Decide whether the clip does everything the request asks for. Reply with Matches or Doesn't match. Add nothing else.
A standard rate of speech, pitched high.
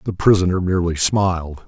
Doesn't match